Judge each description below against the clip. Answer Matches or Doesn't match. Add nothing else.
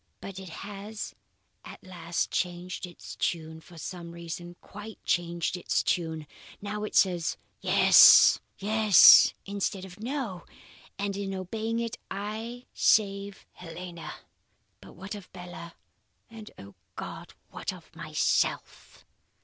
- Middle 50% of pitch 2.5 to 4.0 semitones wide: Matches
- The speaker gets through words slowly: Matches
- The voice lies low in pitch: Doesn't match